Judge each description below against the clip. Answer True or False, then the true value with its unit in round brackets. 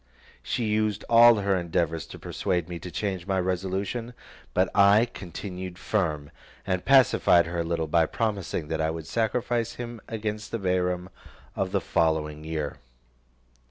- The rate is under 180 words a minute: True (155 wpm)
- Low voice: True (95 Hz)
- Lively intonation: False (4.3 semitones)